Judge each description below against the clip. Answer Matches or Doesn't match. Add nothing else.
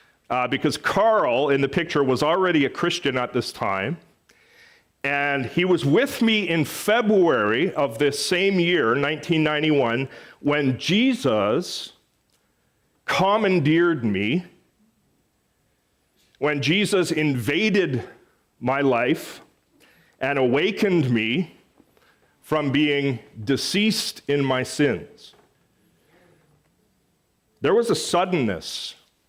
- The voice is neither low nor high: Matches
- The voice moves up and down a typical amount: Matches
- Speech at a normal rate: Doesn't match